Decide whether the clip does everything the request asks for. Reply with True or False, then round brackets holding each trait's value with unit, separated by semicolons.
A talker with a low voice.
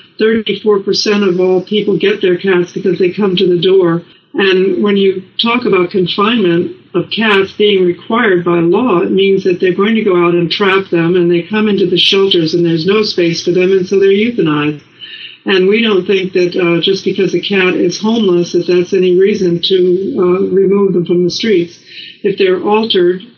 False (190 Hz)